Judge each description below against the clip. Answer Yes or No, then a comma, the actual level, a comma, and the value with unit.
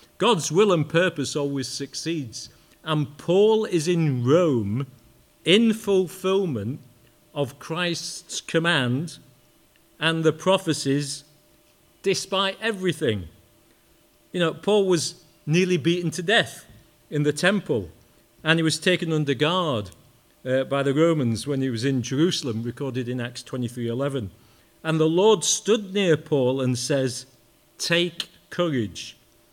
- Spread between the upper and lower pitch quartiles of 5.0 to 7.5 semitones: Yes, wide, 5.4 semitones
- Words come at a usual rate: No, slow, 125 wpm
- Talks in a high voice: No, medium, 150 Hz